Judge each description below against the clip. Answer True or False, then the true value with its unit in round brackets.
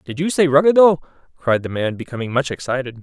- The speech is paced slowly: False (200 wpm)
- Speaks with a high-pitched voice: False (140 Hz)